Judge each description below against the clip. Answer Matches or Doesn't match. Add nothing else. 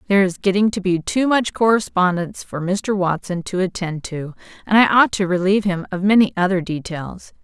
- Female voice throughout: Matches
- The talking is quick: Doesn't match